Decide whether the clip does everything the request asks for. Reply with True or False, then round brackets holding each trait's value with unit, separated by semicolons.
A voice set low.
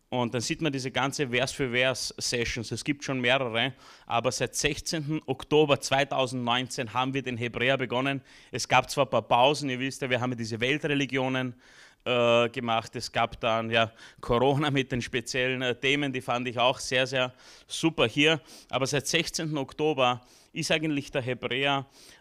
True (130 Hz)